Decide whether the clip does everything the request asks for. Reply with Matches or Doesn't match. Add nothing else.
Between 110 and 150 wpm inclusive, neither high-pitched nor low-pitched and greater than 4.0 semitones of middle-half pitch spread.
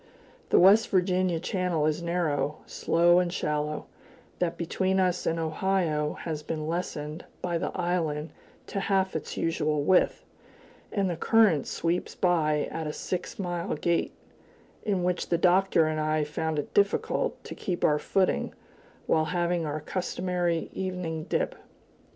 Doesn't match